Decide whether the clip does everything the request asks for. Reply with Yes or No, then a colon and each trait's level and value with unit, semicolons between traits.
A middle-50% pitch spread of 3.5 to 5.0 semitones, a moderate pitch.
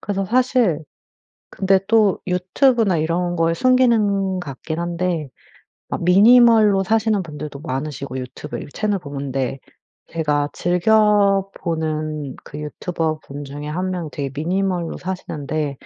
Yes: average, 4.7 semitones; medium, 175 Hz